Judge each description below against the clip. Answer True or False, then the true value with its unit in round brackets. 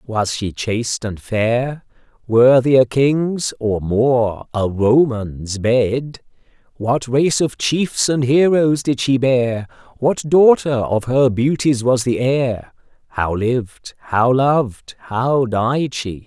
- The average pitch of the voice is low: True (125 Hz)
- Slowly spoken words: True (120 wpm)